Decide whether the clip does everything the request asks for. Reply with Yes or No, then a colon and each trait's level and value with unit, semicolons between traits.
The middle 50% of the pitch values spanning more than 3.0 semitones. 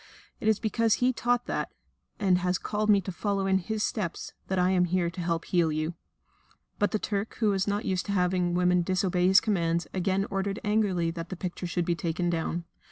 No: average, 2.7 semitones